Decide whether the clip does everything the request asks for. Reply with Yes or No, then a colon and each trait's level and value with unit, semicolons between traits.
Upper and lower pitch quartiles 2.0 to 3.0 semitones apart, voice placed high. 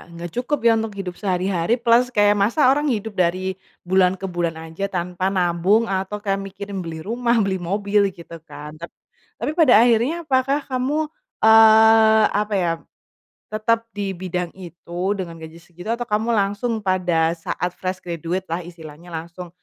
No: average, 4.2 semitones; high, 195 Hz